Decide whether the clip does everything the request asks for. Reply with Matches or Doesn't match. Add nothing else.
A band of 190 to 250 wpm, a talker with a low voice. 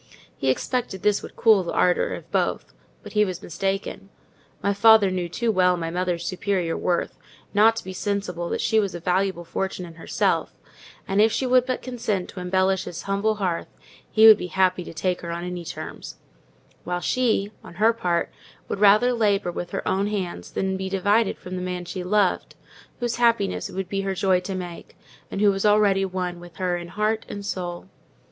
Doesn't match